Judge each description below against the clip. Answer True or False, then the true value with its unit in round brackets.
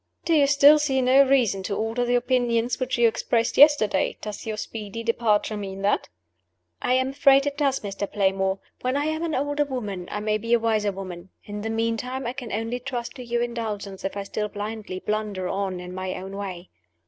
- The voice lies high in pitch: True (225 Hz)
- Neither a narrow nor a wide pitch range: True (4.2 semitones)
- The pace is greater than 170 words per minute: True (205 wpm)